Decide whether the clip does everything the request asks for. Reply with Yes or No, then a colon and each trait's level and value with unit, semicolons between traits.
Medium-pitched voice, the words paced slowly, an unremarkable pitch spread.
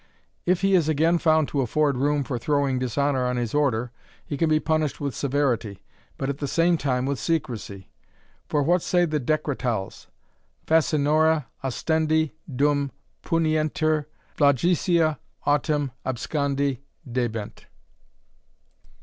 Yes: medium, 145 Hz; slow, 125 wpm; average, 3.2 semitones